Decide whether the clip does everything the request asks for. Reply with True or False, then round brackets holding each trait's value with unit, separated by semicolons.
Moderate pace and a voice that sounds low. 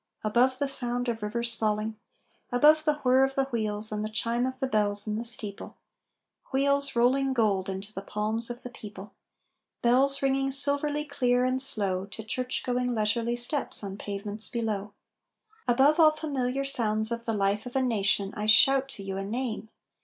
False (175 wpm; 235 Hz)